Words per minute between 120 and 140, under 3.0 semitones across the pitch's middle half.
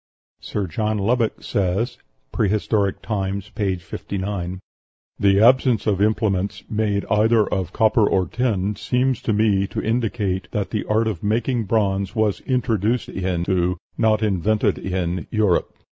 Yes: slow, 135 wpm; narrow, 2.5 semitones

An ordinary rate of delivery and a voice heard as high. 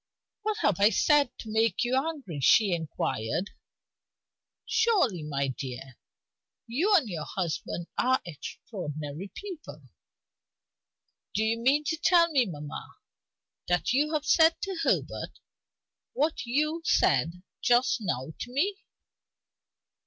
No: slow, 120 wpm; high, 230 Hz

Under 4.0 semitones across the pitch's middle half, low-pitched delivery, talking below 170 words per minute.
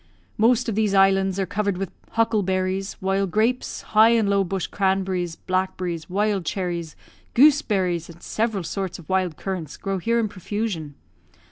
No: average, 2.7 semitones; high, 195 Hz; average, 150 wpm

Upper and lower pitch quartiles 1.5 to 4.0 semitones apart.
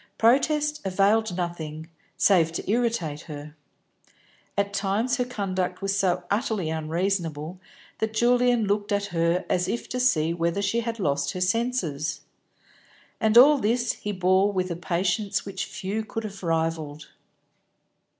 No: average, 4.8 semitones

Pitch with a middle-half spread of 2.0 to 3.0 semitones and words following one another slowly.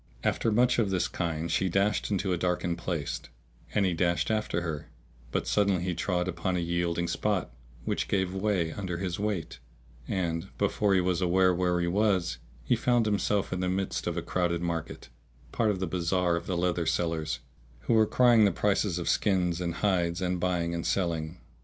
No: narrow, 2.4 semitones; average, 190 wpm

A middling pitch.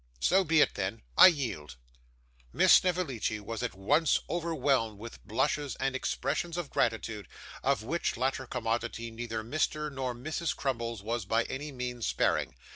No: low, 125 Hz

